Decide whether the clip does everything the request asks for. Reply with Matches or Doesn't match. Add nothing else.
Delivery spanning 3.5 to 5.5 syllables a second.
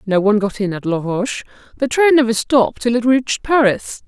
Doesn't match